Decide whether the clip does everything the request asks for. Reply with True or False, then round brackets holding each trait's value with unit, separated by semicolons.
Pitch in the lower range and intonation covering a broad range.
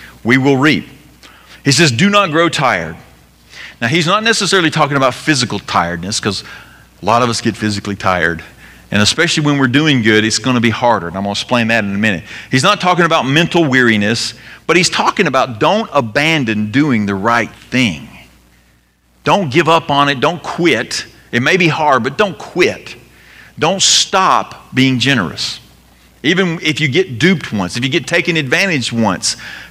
True (125 Hz; 7.2 semitones)